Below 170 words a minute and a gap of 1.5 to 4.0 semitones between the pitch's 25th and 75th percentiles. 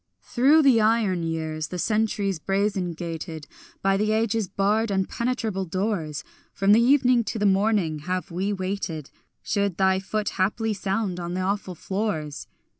Yes: average, 150 wpm; average, 3.3 semitones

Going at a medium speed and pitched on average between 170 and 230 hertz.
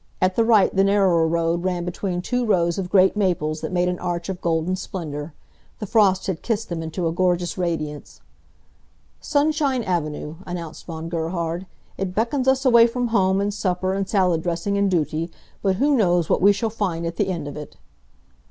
Yes: average, 190 wpm; medium, 185 Hz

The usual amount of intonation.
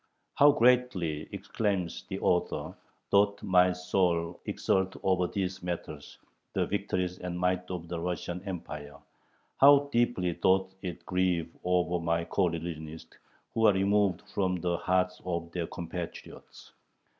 No: narrow, 2.0 semitones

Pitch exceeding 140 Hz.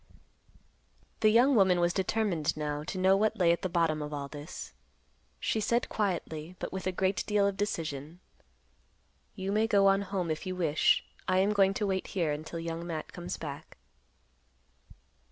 Yes: medium, 185 Hz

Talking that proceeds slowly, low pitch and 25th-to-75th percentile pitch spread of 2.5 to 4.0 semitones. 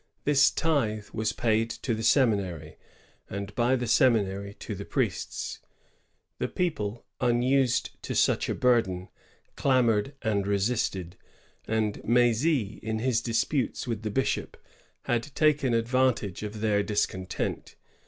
Yes: slow, 125 wpm; low, 115 Hz; average, 3.7 semitones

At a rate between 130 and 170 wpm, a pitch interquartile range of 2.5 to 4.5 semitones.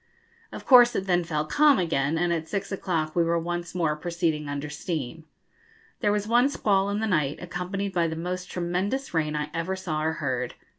No: average, 200 wpm; average, 3.7 semitones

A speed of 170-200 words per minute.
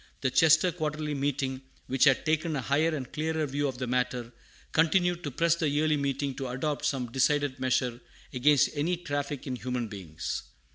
Yes: average, 180 wpm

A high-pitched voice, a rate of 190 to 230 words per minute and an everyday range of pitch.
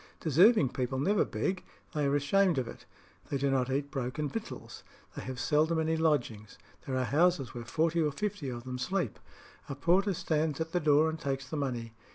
No: medium, 145 Hz; average, 200 wpm; average, 3.8 semitones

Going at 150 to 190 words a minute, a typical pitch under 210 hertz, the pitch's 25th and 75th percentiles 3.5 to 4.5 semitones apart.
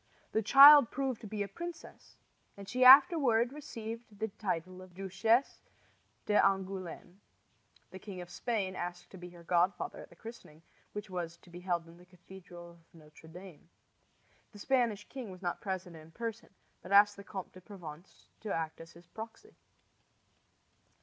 Yes: average, 165 wpm; high, 190 Hz; average, 4.2 semitones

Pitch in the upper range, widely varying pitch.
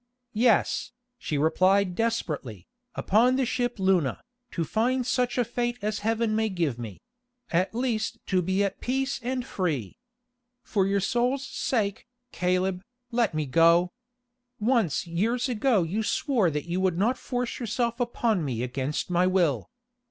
Yes: high, 200 Hz; wide, 5.8 semitones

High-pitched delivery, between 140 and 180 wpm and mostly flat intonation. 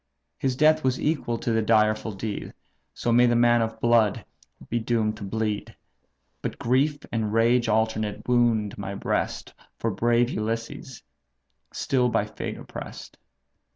No: low, 115 Hz; average, 145 wpm; narrow, 2.0 semitones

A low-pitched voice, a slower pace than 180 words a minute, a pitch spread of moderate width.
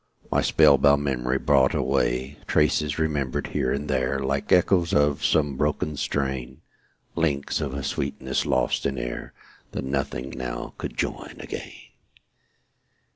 No: very low, 70 Hz; slow, 135 wpm; narrow, 1.9 semitones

